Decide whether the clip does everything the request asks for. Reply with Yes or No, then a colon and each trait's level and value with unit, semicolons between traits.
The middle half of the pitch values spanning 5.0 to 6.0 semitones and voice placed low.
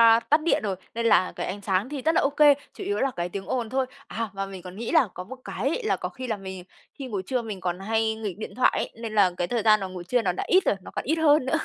No: wide, 5.5 semitones; high, 225 Hz